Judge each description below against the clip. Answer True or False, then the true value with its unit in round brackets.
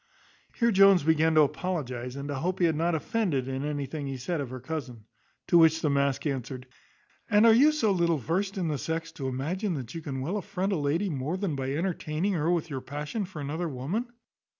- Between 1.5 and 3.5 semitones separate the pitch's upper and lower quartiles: False (4.9 semitones)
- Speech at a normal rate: False (220 wpm)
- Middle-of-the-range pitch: True (160 Hz)